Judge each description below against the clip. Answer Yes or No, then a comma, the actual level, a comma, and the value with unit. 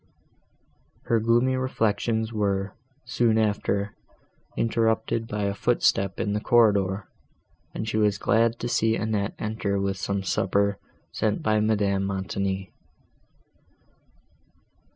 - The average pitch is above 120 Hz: No, low, 105 Hz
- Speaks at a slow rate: Yes, slow, 110 wpm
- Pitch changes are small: Yes, narrow, 2.1 semitones